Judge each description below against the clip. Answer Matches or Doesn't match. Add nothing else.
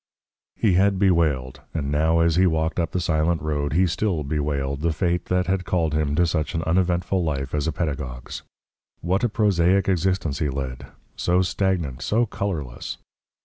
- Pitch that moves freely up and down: Doesn't match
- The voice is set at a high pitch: Doesn't match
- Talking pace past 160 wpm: Matches